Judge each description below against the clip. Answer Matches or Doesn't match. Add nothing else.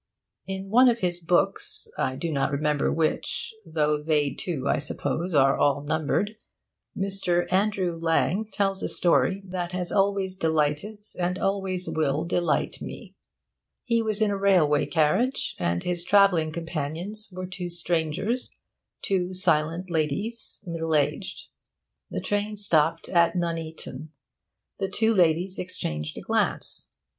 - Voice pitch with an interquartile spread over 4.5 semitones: Doesn't match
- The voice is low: Doesn't match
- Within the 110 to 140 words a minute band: Matches